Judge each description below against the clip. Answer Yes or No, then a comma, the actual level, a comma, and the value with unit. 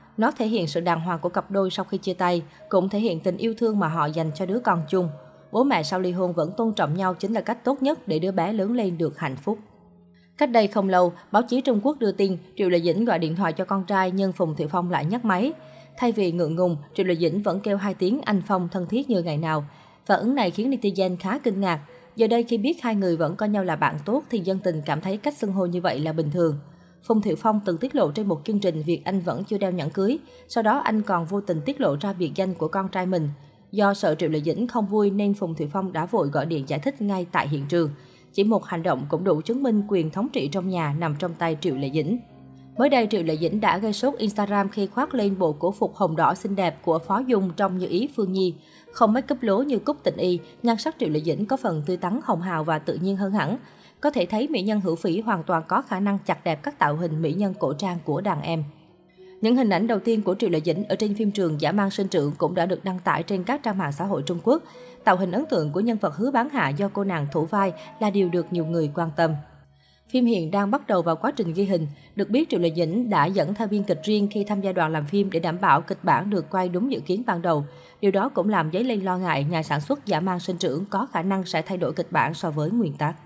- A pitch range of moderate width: Yes, average, 4.2 semitones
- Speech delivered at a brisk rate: Yes, fast, 280 wpm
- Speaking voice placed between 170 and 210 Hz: Yes, high, 190 Hz